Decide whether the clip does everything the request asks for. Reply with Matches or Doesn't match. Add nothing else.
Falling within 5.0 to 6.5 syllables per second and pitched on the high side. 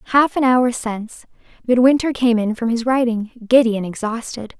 Matches